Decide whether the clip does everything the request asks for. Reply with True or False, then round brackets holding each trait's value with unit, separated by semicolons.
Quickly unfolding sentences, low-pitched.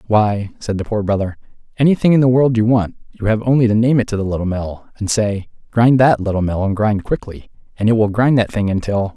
True (235 wpm; 110 Hz)